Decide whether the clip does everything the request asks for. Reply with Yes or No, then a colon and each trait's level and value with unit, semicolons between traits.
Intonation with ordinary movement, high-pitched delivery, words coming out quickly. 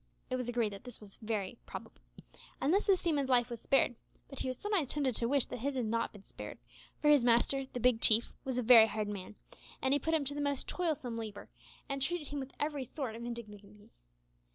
Yes: average, 3.9 semitones; very high, 250 Hz; fast, 225 wpm